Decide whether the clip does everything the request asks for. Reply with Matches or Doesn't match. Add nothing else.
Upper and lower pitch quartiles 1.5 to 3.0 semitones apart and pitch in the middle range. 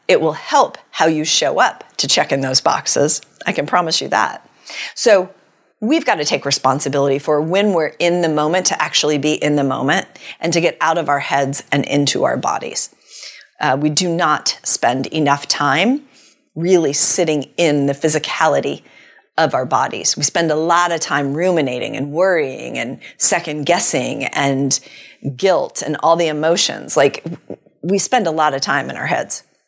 Doesn't match